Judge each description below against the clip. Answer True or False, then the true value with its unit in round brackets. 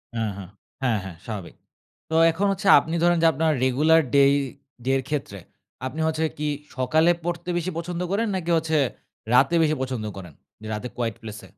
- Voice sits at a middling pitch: True (150 Hz)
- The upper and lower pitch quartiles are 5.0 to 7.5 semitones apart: True (5.3 semitones)